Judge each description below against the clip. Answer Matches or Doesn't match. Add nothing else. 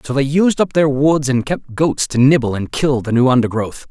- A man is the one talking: Matches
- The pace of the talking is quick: Matches